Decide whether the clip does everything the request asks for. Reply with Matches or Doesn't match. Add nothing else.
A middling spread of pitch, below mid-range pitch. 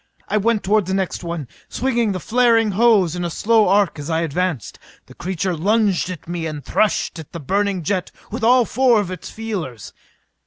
Doesn't match